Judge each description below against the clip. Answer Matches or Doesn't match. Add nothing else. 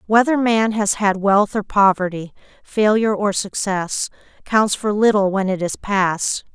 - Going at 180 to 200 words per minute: Doesn't match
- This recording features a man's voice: Doesn't match